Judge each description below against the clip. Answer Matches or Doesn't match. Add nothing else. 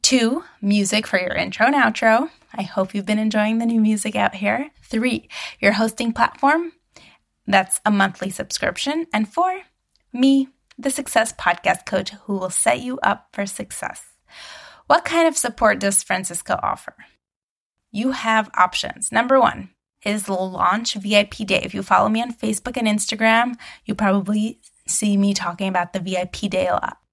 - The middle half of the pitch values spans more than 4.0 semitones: Doesn't match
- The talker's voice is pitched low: Doesn't match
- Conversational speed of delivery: Matches